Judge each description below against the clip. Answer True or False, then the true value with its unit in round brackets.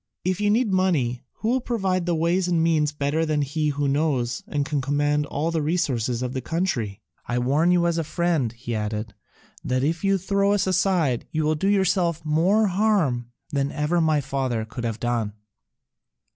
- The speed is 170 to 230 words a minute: True (190 wpm)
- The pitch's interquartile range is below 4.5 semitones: False (5.6 semitones)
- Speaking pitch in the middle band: True (155 Hz)